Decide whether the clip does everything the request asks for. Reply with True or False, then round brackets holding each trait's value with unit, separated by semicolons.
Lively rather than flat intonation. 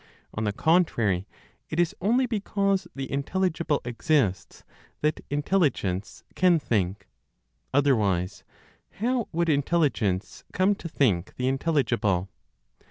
True (8.9 semitones)